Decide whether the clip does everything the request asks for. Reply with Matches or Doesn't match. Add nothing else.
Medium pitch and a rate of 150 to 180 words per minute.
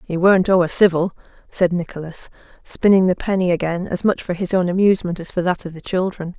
Doesn't match